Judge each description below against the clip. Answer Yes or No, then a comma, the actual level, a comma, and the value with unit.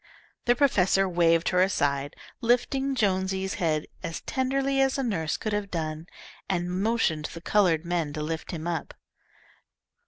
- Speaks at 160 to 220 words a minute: No, average, 150 wpm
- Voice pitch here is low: No, medium, 185 Hz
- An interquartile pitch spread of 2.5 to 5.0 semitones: No, wide, 5.6 semitones